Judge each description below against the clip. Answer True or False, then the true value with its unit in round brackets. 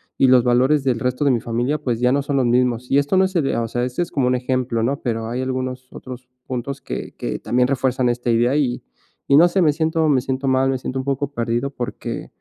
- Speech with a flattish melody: True (2.2 semitones)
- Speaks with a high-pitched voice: False (130 Hz)